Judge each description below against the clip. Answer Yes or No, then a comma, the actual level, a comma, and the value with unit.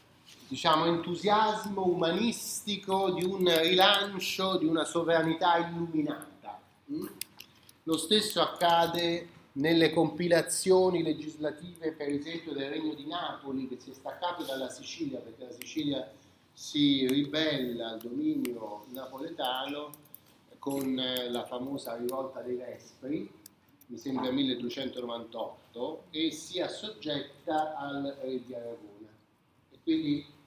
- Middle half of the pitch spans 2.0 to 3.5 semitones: No, average, 4.6 semitones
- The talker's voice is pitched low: No, medium, 155 Hz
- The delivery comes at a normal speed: No, slow, 105 wpm